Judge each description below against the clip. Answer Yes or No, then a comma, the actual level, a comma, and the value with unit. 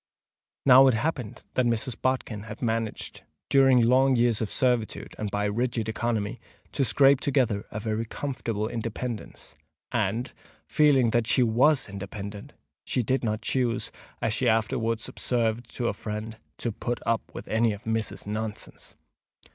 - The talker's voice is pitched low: Yes, low, 115 Hz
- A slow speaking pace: No, average, 150 wpm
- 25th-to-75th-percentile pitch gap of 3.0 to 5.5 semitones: No, narrow, 2.5 semitones